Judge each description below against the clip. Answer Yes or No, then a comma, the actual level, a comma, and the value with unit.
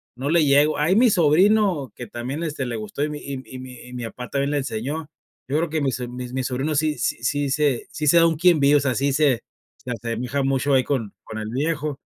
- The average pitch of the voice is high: No, medium, 140 Hz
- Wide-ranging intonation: No, average, 3.2 semitones